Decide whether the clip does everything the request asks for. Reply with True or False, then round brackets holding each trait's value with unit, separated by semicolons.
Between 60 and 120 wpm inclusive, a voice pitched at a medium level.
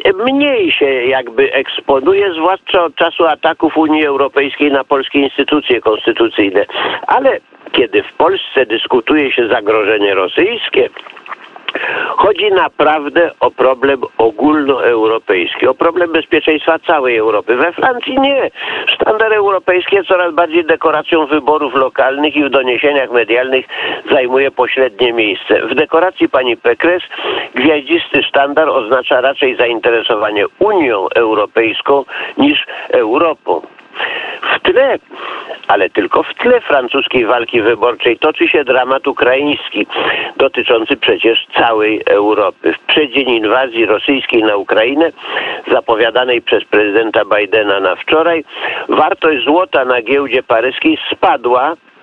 True (110 wpm; 165 Hz)